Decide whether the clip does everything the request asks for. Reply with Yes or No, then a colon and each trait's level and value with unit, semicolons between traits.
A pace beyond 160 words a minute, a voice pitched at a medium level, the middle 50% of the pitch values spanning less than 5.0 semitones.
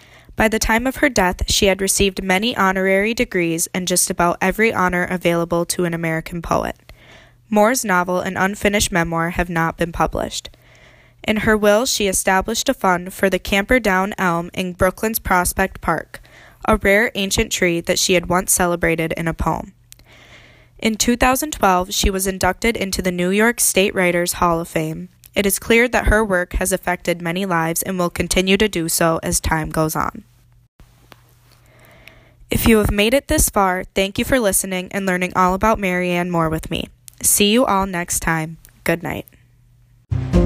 Yes: average, 175 wpm; medium, 180 Hz; average, 3.2 semitones